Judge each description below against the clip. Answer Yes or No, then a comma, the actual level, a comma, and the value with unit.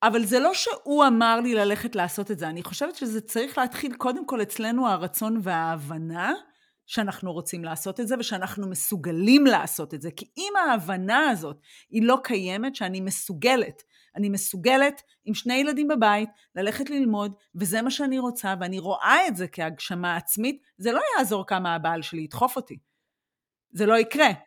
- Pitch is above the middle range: Yes, high, 215 Hz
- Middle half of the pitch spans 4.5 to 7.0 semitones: Yes, wide, 5.5 semitones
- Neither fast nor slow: No, fast, 165 wpm